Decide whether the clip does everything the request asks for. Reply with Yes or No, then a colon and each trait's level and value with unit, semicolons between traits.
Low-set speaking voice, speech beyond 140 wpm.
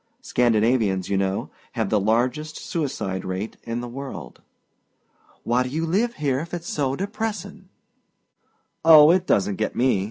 Yes: low, 130 Hz; average, 150 wpm